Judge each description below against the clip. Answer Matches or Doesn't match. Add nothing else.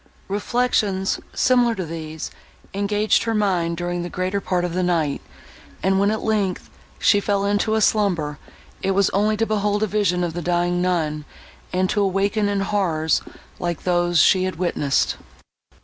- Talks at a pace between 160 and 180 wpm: Matches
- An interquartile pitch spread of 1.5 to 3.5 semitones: Matches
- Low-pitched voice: Doesn't match